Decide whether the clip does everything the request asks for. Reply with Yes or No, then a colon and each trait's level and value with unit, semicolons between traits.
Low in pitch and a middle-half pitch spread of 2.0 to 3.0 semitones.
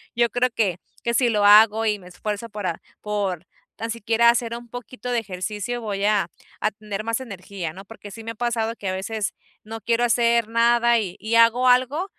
No: high, 225 Hz; narrow, 2.5 semitones